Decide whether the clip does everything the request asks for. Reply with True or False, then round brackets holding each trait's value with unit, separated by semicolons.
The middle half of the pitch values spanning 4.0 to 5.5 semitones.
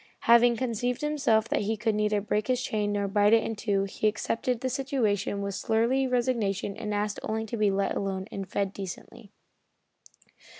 False (2.7 semitones)